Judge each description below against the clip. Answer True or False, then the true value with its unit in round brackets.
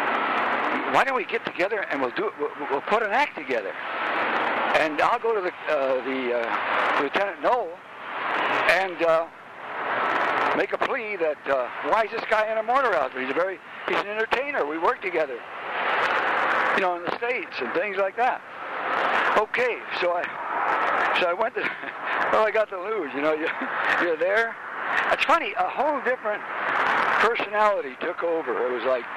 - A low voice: False (205 Hz)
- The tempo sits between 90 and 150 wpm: False (175 wpm)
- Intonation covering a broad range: True (6.3 semitones)